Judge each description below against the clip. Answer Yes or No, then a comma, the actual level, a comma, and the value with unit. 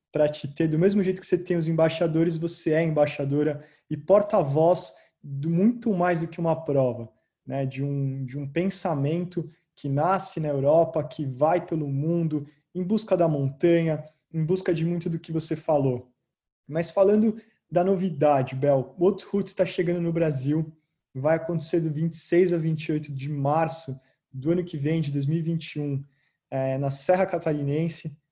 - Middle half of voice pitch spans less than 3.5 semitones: Yes, average, 2.9 semitones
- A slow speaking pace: No, average, 165 wpm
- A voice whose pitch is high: No, medium, 160 Hz